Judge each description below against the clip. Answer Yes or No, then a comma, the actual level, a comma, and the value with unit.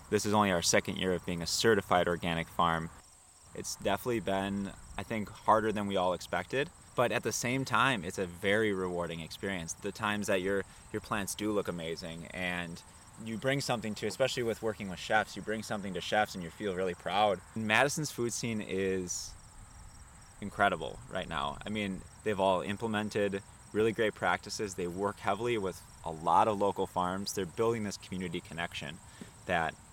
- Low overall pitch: Yes, low, 100 Hz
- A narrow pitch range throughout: No, average, 3.0 semitones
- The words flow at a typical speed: Yes, average, 180 wpm